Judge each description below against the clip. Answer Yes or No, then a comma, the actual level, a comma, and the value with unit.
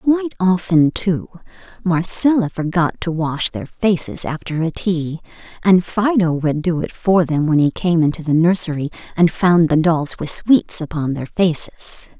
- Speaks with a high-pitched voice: No, medium, 170 Hz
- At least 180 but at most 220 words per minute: No, average, 165 wpm